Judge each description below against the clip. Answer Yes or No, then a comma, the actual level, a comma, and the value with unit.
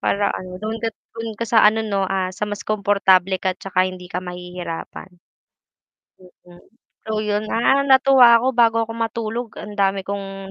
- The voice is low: No, high, 205 Hz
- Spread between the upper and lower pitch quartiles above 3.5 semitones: No, average, 3.2 semitones